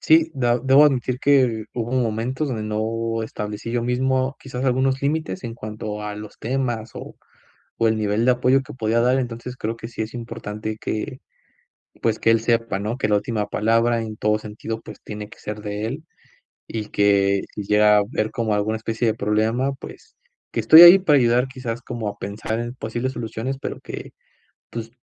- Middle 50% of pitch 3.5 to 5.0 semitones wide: No, average, 2.9 semitones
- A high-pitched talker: No, low, 115 Hz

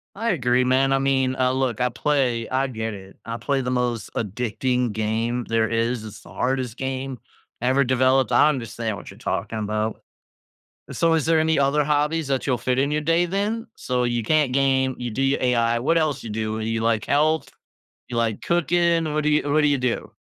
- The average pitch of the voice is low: Yes, low, 130 Hz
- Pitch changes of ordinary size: Yes, average, 3.9 semitones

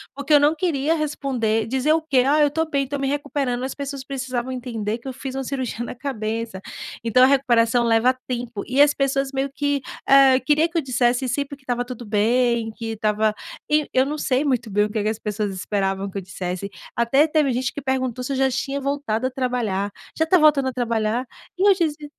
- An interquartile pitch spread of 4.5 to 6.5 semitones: No, average, 3.5 semitones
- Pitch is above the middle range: Yes, very high, 260 Hz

